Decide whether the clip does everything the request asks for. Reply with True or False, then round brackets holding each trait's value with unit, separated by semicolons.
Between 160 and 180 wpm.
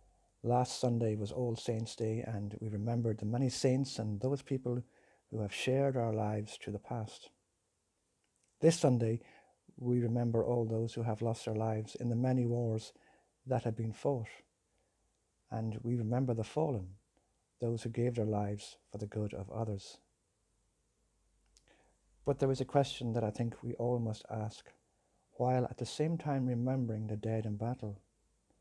True (165 wpm)